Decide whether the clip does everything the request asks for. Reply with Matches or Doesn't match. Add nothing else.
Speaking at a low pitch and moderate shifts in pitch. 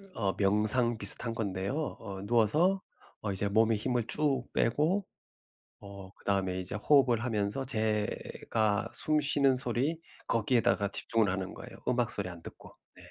Matches